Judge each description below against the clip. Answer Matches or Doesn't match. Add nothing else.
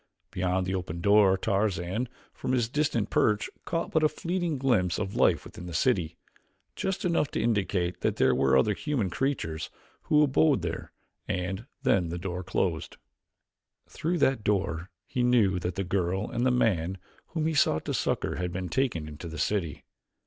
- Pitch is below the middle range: Matches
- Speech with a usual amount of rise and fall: Doesn't match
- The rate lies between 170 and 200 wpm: Matches